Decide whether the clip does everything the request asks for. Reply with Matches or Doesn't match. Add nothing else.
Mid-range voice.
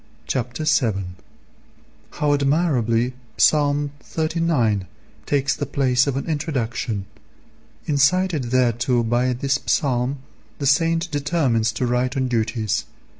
Doesn't match